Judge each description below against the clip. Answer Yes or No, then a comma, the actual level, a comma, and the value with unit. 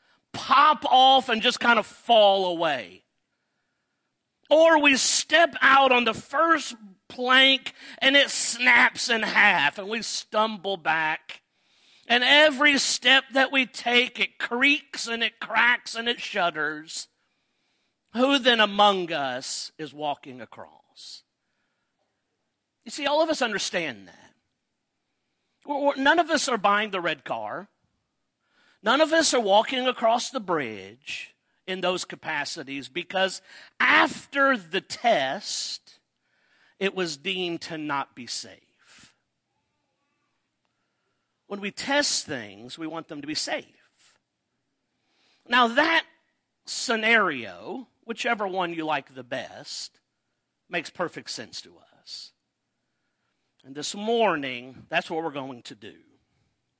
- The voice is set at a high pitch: Yes, high, 230 Hz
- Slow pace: Yes, slow, 125 wpm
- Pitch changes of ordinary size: No, wide, 7.6 semitones